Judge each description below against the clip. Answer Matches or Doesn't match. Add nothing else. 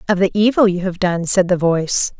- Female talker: Matches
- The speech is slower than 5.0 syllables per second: Doesn't match